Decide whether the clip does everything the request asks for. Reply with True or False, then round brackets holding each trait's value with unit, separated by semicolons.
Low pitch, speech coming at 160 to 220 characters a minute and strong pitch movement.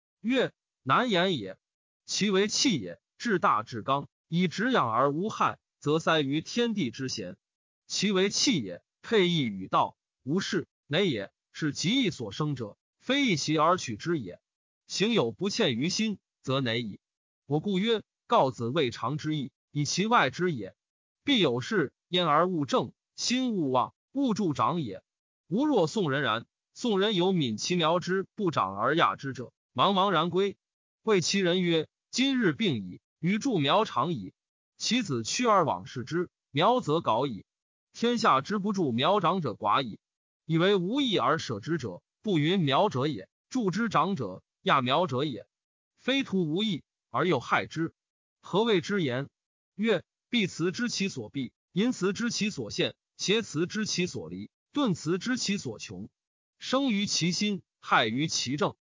False (180 Hz; 215 characters per minute; 6.2 semitones)